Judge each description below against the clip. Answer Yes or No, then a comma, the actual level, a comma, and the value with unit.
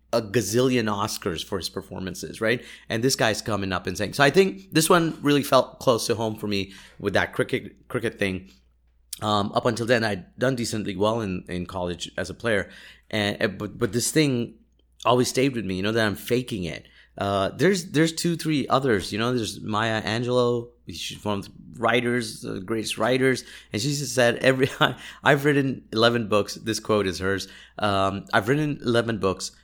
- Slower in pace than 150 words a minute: No, average, 195 wpm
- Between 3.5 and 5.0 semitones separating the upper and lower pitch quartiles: Yes, average, 4.2 semitones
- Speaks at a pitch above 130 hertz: No, low, 110 Hz